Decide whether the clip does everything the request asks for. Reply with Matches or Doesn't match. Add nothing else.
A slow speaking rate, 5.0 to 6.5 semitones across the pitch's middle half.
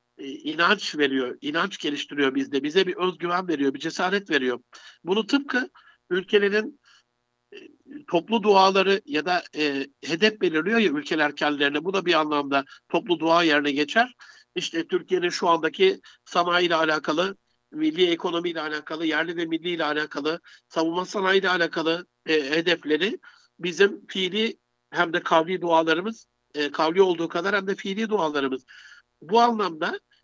Doesn't match